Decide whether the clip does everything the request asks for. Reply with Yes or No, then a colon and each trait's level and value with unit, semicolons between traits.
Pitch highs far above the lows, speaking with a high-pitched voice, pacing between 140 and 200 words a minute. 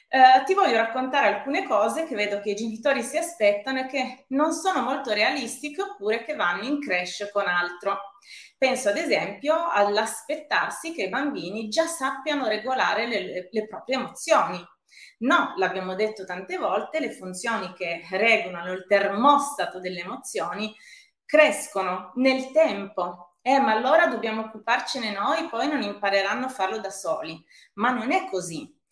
Yes: wide, 6.0 semitones; high, 225 Hz; average, 150 wpm